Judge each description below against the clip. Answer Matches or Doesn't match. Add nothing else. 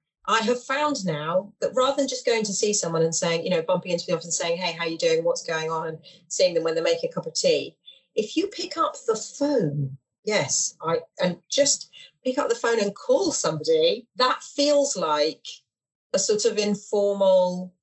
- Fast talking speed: Matches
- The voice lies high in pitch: Matches